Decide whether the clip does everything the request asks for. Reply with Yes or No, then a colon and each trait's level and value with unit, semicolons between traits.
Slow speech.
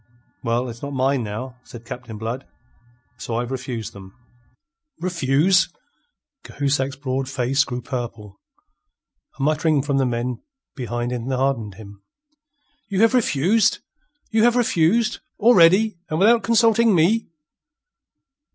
Yes: slow, 120 wpm